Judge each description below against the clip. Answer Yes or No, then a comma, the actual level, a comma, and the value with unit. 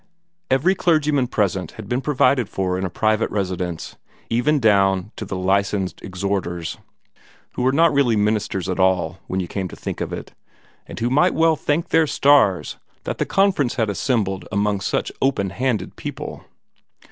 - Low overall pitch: Yes, low, 105 Hz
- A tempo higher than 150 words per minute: Yes, average, 170 wpm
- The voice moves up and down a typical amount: No, wide, 6.2 semitones